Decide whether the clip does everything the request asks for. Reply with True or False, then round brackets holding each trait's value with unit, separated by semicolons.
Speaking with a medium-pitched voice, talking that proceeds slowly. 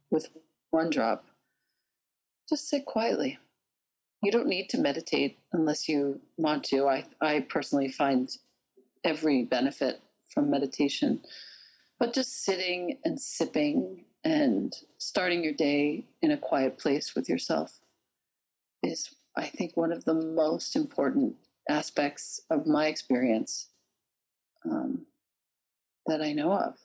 True (170 Hz; 125 wpm)